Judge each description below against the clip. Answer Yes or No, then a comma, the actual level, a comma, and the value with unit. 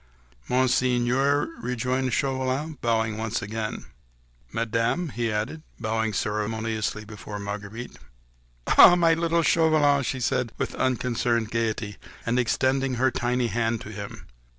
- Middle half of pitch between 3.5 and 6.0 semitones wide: No, average, 3.0 semitones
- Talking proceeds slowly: Yes, slow, 120 wpm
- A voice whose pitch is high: No, low, 120 Hz